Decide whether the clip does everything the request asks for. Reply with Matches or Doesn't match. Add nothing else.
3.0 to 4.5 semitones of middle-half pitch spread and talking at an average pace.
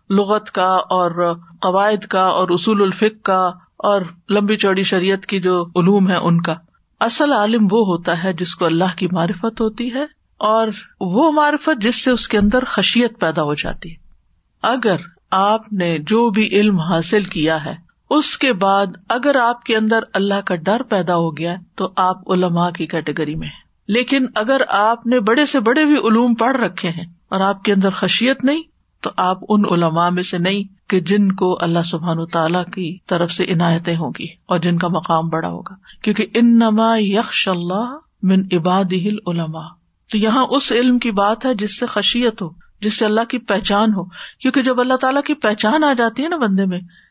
Doesn't match